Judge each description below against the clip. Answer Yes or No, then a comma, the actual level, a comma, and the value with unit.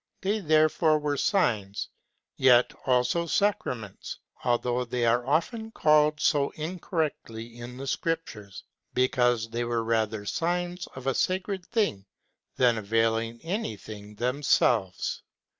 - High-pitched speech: No, low, 125 Hz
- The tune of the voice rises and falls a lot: Yes, wide, 6.1 semitones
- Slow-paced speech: Yes, slow, 115 wpm